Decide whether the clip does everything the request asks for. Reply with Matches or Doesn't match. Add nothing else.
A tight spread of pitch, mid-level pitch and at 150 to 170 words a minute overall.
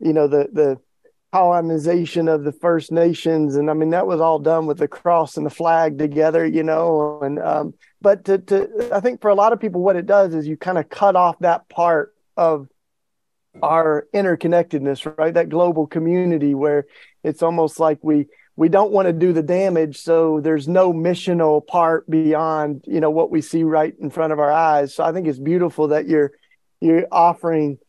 Doesn't match